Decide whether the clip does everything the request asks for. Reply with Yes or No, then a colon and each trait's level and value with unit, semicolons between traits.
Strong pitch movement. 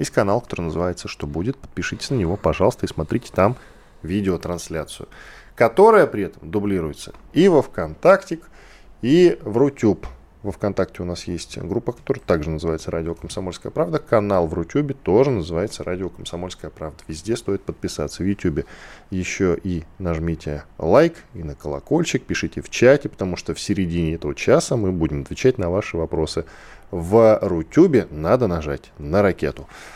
No: average, 4.1 semitones